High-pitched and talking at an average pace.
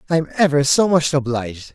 No: medium, 145 Hz; average, 170 wpm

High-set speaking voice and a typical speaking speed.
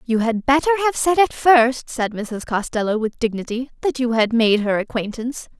Yes: high, 245 Hz; average, 195 wpm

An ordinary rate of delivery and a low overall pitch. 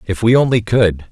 No: fast, 215 wpm; low, 110 Hz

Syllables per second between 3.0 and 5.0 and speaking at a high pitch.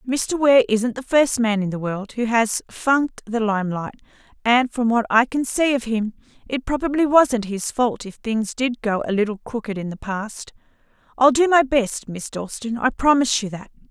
Yes: 4.8 syllables/s; high, 235 Hz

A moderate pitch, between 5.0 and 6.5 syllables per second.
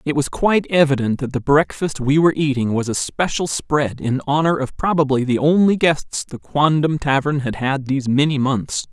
Yes: medium, 145 Hz; 5.1 syllables/s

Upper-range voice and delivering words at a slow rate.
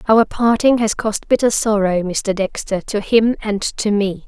No: high, 210 Hz; average, 180 wpm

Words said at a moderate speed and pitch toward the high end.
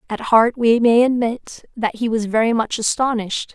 Yes: average, 185 wpm; high, 230 Hz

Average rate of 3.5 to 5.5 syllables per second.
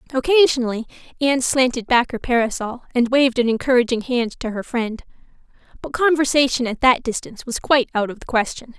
No: 6.1 syllables/s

